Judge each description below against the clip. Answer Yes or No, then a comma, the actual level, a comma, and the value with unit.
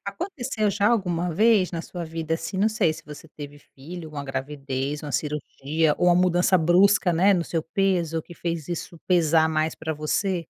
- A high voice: No, medium, 165 Hz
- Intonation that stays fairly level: No, average, 3.3 semitones